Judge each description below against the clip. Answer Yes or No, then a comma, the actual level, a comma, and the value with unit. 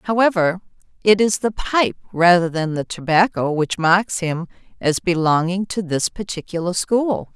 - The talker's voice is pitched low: No, medium, 185 Hz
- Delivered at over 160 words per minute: No, average, 145 wpm